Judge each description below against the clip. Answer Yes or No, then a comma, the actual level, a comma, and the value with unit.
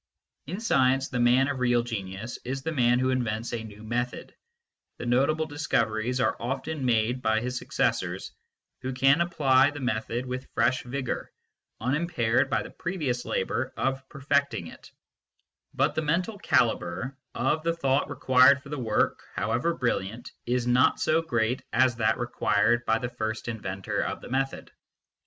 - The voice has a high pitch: No, low, 125 Hz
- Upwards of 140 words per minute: Yes, average, 160 wpm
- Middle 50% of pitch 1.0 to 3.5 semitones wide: Yes, average, 2.9 semitones